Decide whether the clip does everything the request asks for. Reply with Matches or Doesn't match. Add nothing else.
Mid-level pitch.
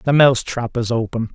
Doesn't match